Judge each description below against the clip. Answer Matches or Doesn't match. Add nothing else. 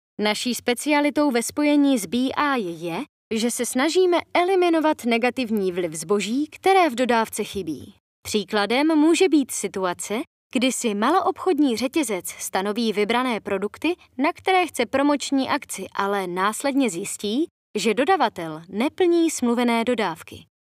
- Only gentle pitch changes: Doesn't match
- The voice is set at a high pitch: Matches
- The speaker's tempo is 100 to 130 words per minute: Matches